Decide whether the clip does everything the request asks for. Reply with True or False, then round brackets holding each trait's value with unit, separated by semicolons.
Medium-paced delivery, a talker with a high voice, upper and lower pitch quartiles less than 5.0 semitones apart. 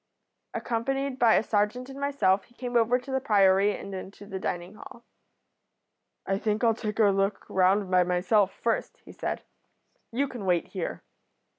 True (170 wpm; 210 Hz; 4.2 semitones)